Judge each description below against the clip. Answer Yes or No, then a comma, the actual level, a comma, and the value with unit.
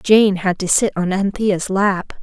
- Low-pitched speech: No, high, 195 Hz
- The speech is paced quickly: No, average, 190 wpm